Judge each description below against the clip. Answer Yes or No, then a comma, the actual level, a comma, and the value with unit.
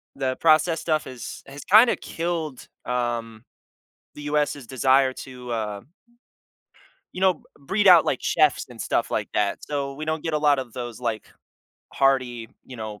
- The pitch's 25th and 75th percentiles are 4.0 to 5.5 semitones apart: Yes, average, 4.3 semitones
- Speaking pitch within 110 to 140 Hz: Yes, low, 135 Hz